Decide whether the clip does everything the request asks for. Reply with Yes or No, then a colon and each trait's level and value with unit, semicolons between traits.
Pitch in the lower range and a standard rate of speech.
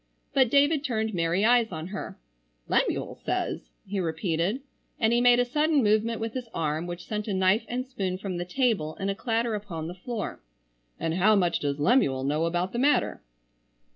No: high, 210 Hz; average, 190 wpm